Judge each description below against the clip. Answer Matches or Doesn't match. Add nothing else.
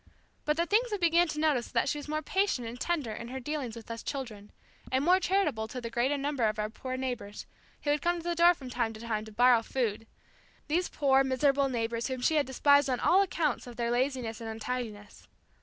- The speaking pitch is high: Matches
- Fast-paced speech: Matches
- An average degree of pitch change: Matches